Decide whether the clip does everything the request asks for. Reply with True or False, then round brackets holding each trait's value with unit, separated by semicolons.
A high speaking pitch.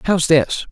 False (160 Hz)